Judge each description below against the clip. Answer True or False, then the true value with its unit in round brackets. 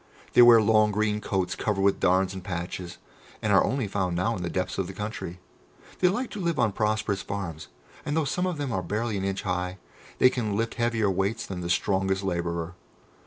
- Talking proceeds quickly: True (215 wpm)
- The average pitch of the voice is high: False (100 Hz)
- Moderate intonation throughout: True (3.6 semitones)